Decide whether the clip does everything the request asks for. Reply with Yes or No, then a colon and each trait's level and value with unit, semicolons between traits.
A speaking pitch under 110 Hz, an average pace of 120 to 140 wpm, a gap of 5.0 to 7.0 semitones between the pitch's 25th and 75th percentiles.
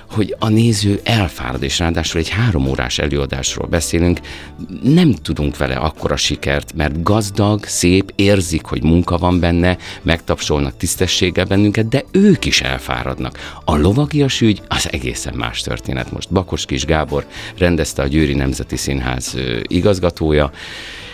Yes: very low, 85 Hz; average, 135 wpm; wide, 5.6 semitones